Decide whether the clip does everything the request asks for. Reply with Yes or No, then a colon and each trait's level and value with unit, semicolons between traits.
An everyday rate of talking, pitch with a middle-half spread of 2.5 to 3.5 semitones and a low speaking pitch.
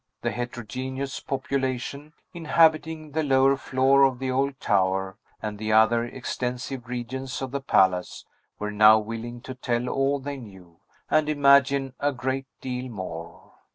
Yes: average, 145 wpm; average, 3.2 semitones; low, 130 Hz